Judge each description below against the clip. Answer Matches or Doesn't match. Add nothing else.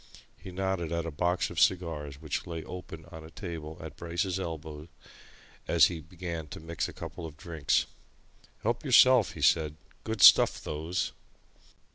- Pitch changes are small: Matches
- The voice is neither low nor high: Doesn't match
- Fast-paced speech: Doesn't match